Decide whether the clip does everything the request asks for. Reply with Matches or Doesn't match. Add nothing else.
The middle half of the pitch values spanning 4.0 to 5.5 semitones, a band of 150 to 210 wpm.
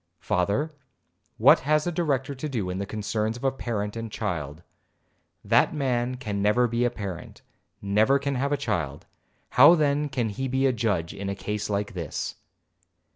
Matches